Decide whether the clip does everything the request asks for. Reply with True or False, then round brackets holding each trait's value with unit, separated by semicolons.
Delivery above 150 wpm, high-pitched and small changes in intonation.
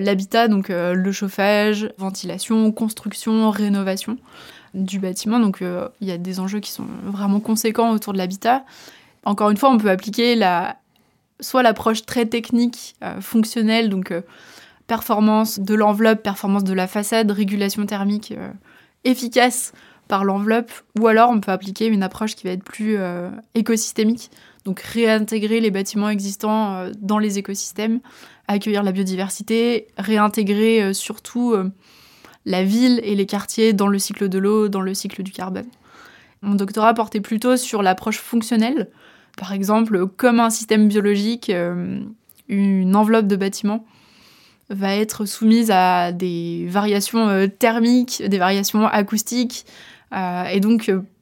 False (145 wpm; 210 Hz; 2.3 semitones)